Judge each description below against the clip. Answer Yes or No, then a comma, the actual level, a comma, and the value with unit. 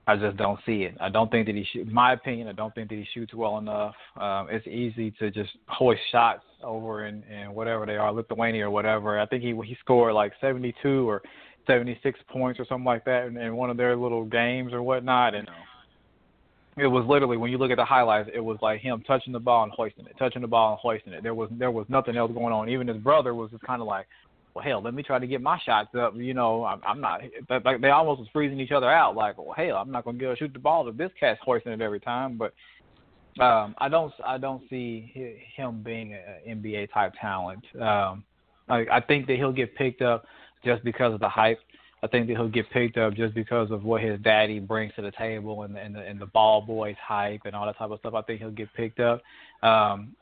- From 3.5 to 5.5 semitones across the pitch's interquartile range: No, narrow, 2.6 semitones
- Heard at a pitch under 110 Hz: No, low, 115 Hz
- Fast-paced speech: Yes, fast, 255 wpm